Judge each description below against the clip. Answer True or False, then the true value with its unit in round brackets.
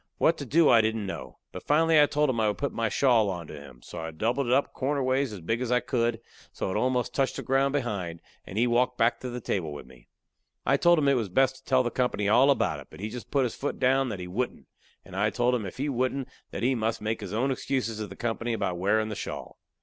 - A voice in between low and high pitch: False (120 Hz)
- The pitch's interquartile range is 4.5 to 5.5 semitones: False (4.0 semitones)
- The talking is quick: True (270 wpm)